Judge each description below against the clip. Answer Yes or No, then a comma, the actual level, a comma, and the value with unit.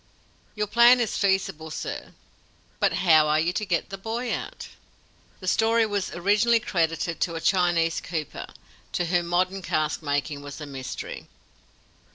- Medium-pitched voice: Yes, medium, 175 Hz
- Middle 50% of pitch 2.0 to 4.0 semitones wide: No, average, 4.6 semitones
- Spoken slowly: No, average, 150 wpm